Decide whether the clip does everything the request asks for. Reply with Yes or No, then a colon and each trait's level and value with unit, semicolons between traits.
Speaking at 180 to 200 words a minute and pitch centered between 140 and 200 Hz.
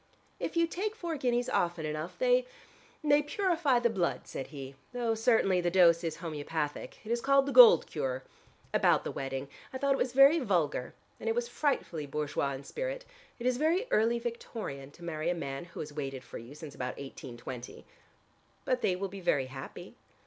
Yes: average, 190 wpm; high, 190 Hz